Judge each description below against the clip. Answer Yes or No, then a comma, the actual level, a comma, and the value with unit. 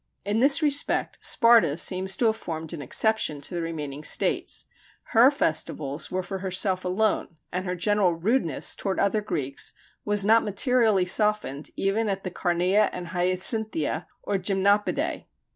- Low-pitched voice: No, high, 190 Hz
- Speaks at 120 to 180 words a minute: Yes, average, 150 wpm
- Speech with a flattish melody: No, average, 3.7 semitones